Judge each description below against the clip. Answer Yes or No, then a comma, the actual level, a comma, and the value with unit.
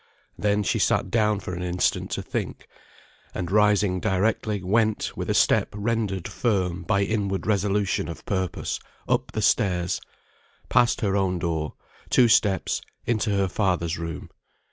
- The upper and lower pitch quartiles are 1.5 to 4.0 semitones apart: Yes, average, 2.7 semitones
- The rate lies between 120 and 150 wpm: Yes, average, 145 wpm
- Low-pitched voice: Yes, low, 100 Hz